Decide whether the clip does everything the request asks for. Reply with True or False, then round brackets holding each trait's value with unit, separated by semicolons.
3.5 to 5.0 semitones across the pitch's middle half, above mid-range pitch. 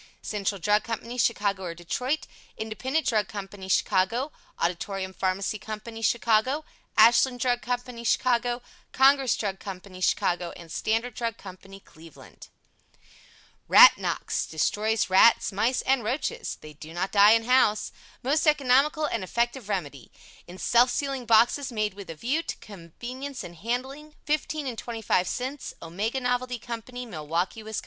True (4.5 semitones; 225 Hz)